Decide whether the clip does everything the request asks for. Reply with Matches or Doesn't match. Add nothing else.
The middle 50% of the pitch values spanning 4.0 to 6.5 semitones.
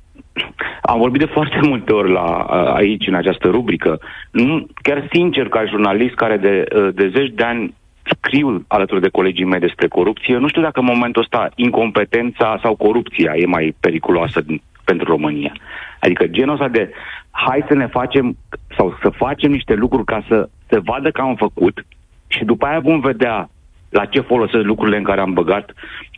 Matches